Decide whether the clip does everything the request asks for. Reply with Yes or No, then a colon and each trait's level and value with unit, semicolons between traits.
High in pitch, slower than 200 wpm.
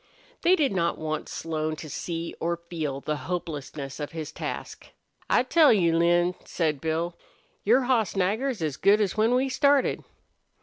No: medium, 170 Hz; average, 165 wpm